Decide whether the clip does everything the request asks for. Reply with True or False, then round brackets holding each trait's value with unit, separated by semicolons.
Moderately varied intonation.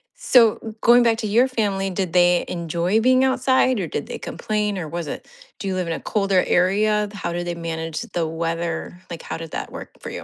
True (4.2 semitones)